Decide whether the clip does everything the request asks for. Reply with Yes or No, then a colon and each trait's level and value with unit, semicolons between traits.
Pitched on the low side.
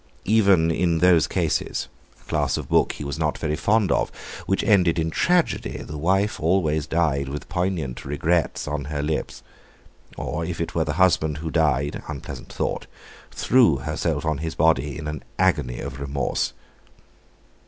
Yes: very low, 80 Hz